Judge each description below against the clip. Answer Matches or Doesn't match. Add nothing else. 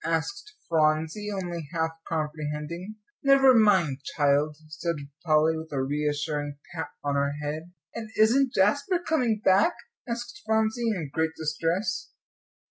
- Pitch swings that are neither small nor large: Doesn't match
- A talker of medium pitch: Matches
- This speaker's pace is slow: Matches